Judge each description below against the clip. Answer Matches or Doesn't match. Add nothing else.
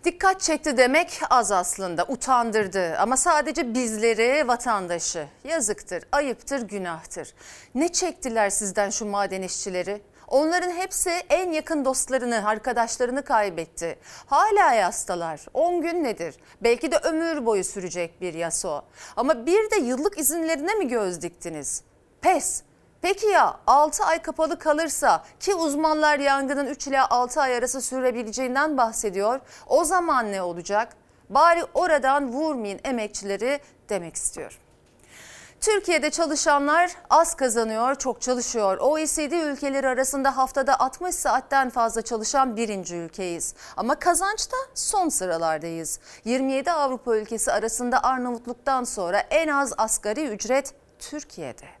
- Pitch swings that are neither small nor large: Doesn't match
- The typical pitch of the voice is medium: Doesn't match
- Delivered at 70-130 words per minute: Matches